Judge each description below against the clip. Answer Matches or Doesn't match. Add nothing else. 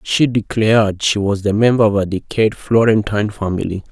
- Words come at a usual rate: Matches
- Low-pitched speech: Matches